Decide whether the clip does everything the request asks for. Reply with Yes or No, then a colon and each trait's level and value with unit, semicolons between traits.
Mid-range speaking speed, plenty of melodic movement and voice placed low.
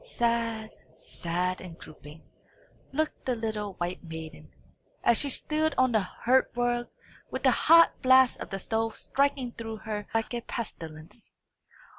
No: average, 145 wpm; wide, 5.7 semitones; high, 225 Hz